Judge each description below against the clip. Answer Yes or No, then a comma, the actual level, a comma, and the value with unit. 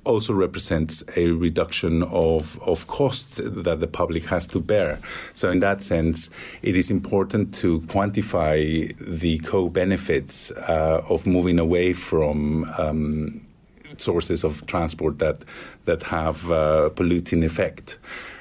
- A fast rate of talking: No, slow, 135 wpm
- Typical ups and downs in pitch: No, narrow, 2.1 semitones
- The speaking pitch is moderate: No, very low, 85 Hz